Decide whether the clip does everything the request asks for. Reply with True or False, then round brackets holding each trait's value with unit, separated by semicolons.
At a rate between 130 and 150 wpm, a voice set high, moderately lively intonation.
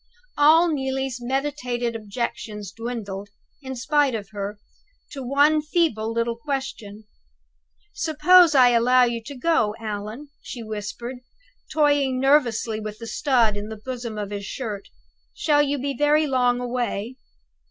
True (135 wpm; 245 Hz; 4.4 semitones)